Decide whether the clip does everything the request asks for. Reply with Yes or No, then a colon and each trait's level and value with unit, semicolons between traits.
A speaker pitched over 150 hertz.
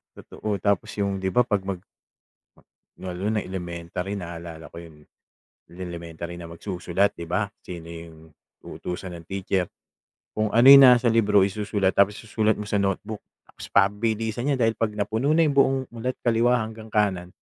No: low, 100 Hz